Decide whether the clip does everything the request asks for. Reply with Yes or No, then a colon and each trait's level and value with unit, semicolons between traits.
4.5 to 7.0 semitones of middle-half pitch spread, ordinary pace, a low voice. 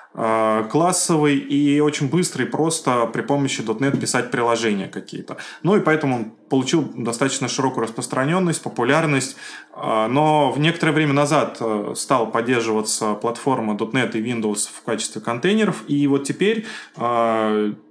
Yes: average, 4.8 semitones; average, 125 wpm; low, 130 Hz